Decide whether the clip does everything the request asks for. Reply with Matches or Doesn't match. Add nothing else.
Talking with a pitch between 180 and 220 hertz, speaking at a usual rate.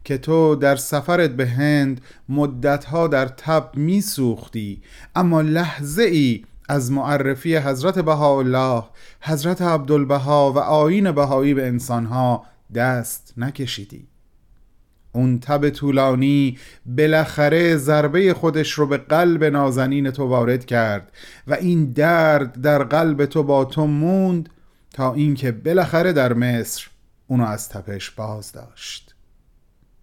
Doesn't match